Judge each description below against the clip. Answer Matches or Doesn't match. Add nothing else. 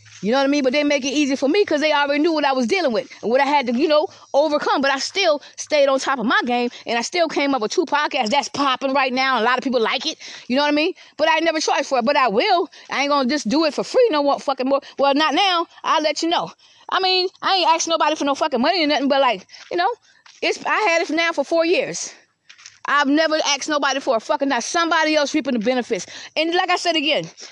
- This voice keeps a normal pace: Doesn't match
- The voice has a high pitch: Matches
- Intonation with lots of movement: Doesn't match